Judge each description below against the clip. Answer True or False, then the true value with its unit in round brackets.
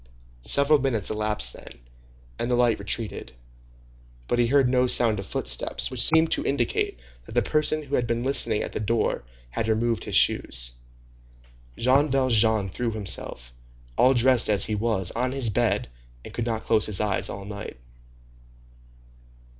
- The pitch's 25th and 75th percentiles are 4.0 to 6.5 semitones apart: False (3.4 semitones)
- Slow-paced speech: False (160 wpm)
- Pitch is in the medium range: False (115 Hz)